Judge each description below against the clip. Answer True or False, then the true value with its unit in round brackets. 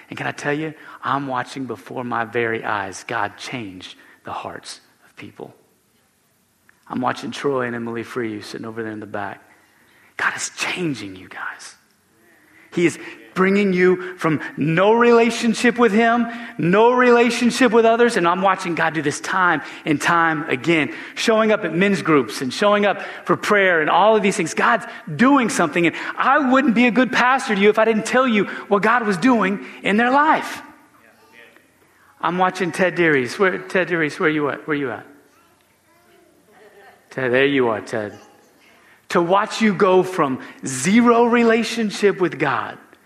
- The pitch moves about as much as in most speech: False (7.3 semitones)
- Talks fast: False (175 wpm)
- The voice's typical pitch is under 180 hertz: False (190 Hz)